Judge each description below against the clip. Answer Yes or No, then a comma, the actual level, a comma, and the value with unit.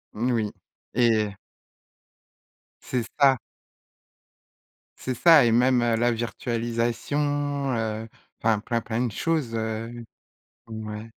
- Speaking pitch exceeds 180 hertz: No, low, 120 Hz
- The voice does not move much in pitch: Yes, narrow, 2.3 semitones